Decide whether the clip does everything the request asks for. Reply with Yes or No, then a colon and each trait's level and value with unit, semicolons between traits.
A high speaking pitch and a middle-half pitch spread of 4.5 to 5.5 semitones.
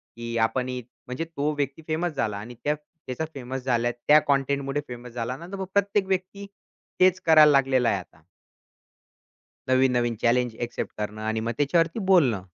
No: low, 135 Hz; average, 4.9 semitones